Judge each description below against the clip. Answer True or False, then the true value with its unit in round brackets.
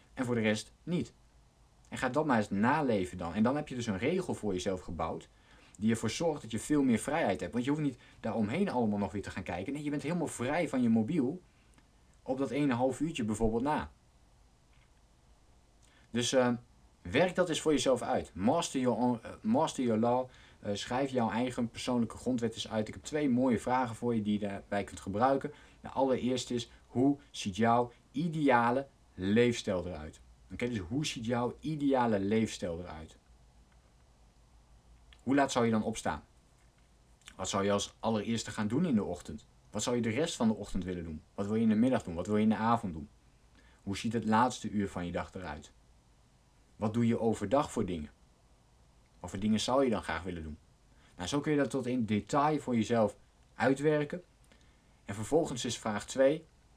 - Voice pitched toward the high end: False (110 Hz)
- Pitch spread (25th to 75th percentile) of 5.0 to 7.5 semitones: True (5.6 semitones)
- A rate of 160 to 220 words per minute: True (200 wpm)